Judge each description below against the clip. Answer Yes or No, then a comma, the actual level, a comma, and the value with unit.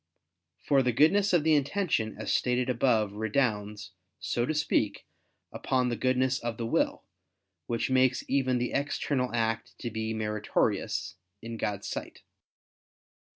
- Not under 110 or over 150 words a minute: Yes, average, 140 wpm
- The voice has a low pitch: Yes, low, 125 Hz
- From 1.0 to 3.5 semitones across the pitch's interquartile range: Yes, average, 3.2 semitones